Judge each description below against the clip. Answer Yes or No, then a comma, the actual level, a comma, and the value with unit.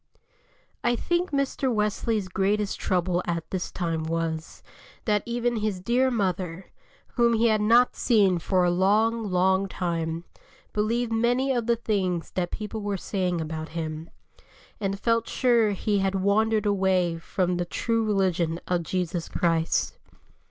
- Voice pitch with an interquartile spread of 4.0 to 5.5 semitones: Yes, average, 4.3 semitones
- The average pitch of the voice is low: No, high, 195 Hz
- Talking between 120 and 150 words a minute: Yes, average, 145 wpm